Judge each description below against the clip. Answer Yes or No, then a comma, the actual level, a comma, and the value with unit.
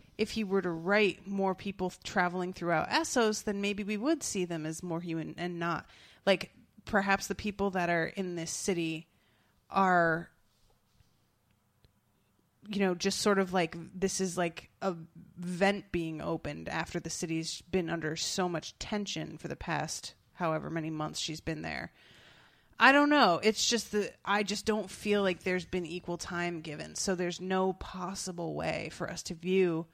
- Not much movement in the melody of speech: No, average, 3.1 semitones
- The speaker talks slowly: No, average, 170 wpm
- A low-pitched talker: No, medium, 180 Hz